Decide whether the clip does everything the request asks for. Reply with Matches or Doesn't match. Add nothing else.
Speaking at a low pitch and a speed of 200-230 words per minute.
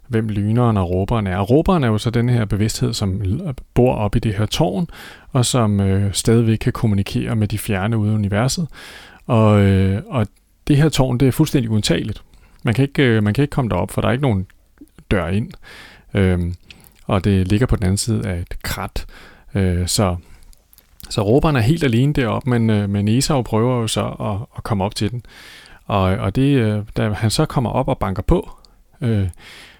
Matches